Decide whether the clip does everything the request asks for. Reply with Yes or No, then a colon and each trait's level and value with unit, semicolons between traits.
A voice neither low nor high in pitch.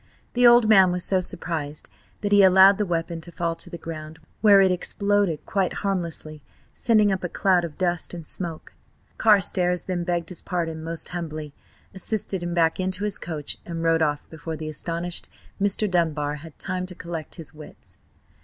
Yes: medium, 175 Hz